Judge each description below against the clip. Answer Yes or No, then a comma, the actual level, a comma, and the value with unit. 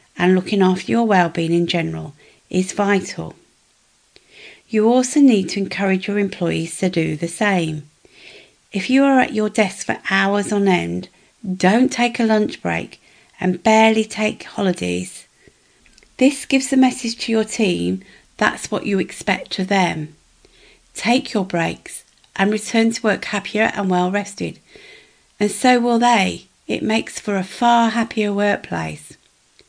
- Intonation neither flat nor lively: Yes, average, 4.2 semitones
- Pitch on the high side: Yes, high, 205 Hz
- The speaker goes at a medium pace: Yes, average, 150 wpm